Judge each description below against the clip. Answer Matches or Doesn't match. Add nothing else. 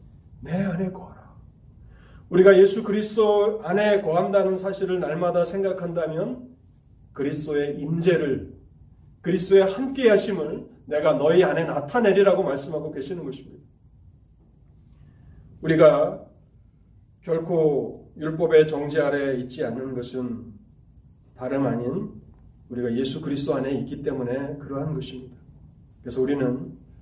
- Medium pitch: Matches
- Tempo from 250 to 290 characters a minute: Matches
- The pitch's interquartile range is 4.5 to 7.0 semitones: Matches